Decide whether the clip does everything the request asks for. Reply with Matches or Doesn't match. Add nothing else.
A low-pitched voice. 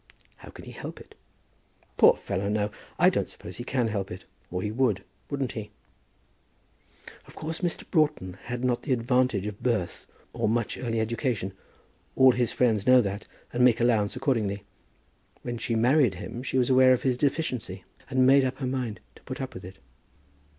Matches